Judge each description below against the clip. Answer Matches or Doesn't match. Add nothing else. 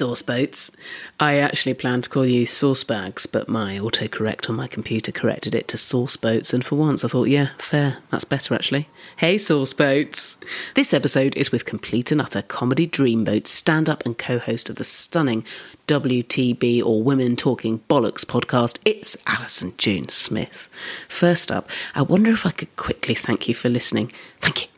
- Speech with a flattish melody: Doesn't match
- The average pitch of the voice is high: Doesn't match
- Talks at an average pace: Matches